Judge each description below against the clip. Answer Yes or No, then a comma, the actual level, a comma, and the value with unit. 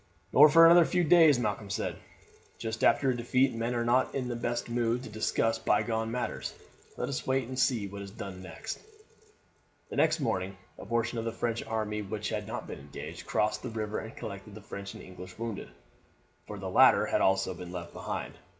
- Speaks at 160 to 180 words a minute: No, fast, 205 wpm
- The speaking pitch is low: Yes, low, 115 Hz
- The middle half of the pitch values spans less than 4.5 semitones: Yes, average, 3.5 semitones